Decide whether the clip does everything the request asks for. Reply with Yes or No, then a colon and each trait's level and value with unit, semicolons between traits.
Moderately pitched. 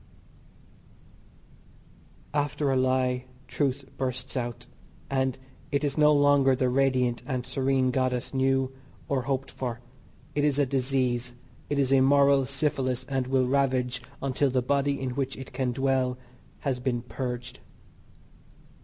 No: low, 130 Hz